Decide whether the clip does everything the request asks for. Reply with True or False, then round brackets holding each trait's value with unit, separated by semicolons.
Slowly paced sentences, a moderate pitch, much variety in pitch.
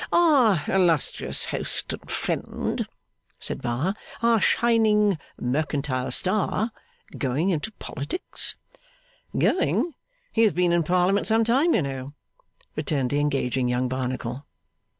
True (115 wpm; 170 Hz; 8.2 semitones)